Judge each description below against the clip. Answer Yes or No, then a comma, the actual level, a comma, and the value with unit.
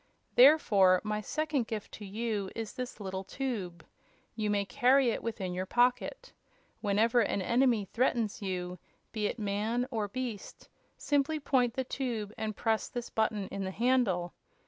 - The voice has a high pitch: Yes, high, 220 Hz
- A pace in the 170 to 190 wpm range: No, average, 155 wpm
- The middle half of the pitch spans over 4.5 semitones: No, average, 3.8 semitones